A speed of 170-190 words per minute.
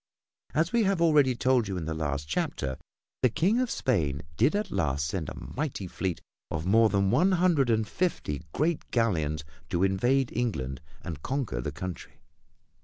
Yes: average, 175 wpm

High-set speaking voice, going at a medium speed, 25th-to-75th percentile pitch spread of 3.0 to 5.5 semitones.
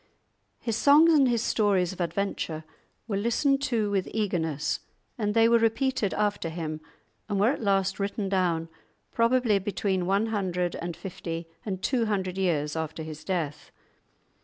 Yes: high, 195 Hz; average, 155 wpm; average, 4.6 semitones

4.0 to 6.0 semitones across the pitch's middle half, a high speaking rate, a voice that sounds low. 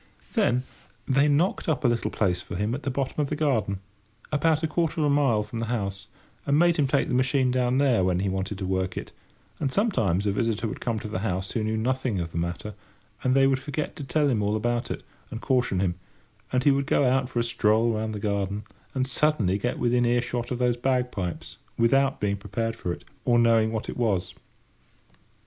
Yes: average, 4.5 semitones; fast, 220 wpm; low, 120 Hz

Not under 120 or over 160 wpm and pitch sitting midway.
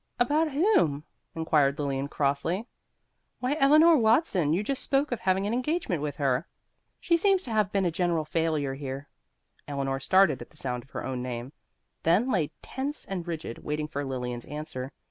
No: average, 175 wpm; medium, 165 Hz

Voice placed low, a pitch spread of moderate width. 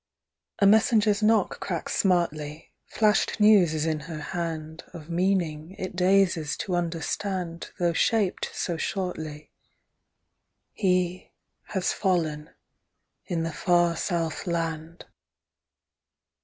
No: medium, 175 Hz; average, 3.0 semitones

